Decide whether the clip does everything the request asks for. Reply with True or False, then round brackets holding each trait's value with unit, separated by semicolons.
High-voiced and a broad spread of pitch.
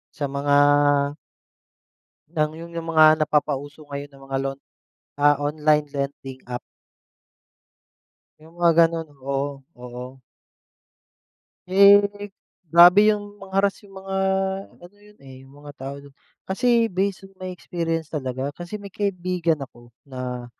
False (155 Hz; 5.7 semitones)